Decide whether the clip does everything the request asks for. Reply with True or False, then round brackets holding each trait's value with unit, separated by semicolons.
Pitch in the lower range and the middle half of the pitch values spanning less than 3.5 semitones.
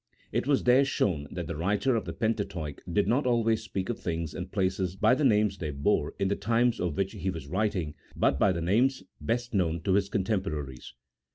False (100 Hz; 5.1 semitones)